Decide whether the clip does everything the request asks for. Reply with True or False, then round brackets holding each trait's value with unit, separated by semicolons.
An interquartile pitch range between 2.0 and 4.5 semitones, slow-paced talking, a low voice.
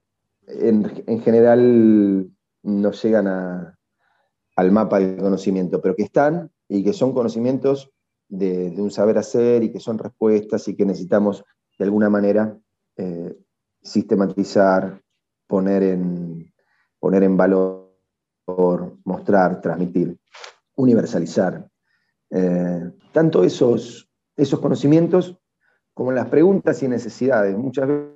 True (3.7 semitones; 115 wpm; 100 Hz)